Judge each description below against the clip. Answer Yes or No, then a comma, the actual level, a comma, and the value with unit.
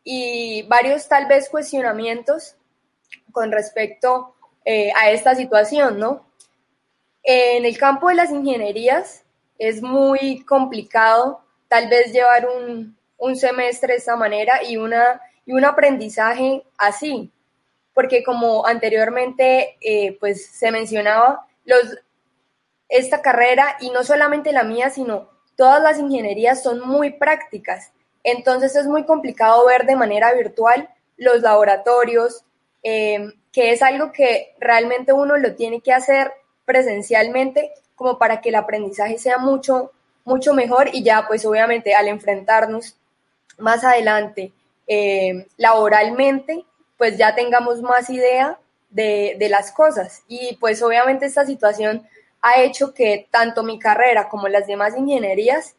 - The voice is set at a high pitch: Yes, high, 245 Hz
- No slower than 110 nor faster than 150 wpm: Yes, average, 130 wpm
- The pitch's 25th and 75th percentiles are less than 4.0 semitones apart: Yes, average, 3.4 semitones